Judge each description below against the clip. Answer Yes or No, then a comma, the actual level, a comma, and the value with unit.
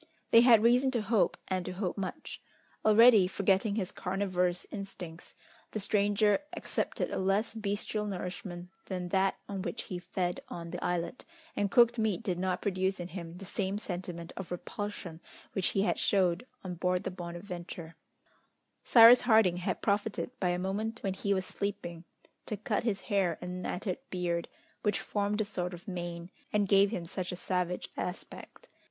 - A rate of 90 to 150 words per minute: No, average, 170 wpm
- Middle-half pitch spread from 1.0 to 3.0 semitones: Yes, narrow, 2.6 semitones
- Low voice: No, high, 190 Hz